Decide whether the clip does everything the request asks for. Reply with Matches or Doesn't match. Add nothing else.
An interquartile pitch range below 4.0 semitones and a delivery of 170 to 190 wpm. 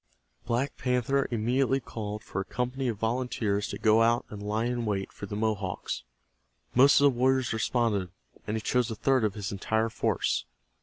Matches